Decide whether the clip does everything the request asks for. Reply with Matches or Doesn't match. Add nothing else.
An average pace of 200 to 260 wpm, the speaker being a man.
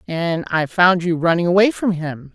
Doesn't match